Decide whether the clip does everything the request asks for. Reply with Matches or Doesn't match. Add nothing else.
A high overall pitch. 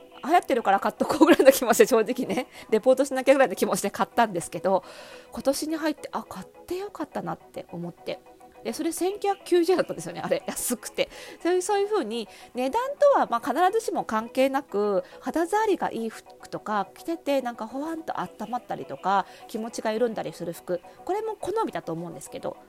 Matches